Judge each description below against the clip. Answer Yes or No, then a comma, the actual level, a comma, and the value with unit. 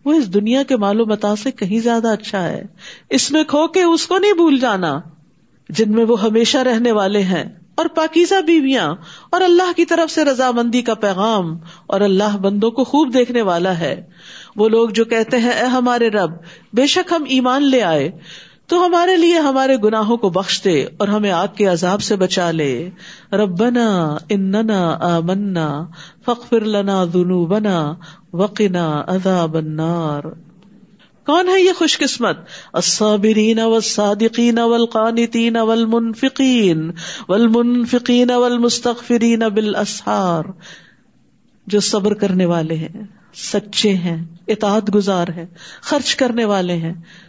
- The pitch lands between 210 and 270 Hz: Yes, high, 215 Hz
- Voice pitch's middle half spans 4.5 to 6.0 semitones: Yes, average, 4.9 semitones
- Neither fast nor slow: Yes, average, 140 wpm